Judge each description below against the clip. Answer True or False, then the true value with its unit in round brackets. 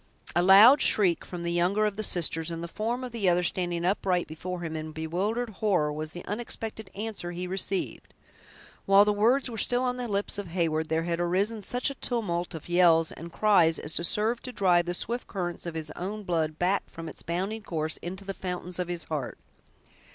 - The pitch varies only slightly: False (3.7 semitones)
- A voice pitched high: False (180 Hz)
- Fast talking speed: True (210 wpm)